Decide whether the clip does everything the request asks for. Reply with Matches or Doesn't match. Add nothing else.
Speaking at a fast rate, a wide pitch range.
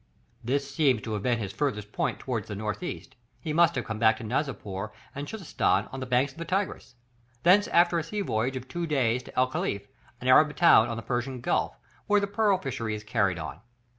Matches